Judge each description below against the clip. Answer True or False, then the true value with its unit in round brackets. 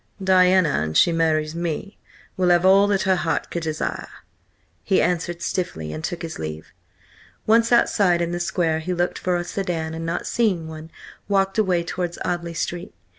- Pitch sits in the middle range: True (175 Hz)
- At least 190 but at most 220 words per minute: False (175 wpm)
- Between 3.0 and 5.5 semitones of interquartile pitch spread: False (2.4 semitones)